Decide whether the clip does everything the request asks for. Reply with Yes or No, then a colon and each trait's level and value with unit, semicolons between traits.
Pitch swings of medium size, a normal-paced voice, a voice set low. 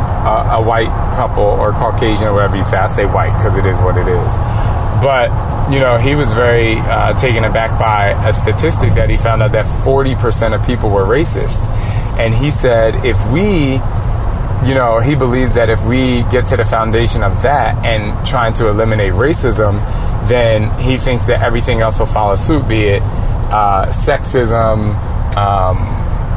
No: narrow, 2.2 semitones; average, 180 wpm; low, 110 Hz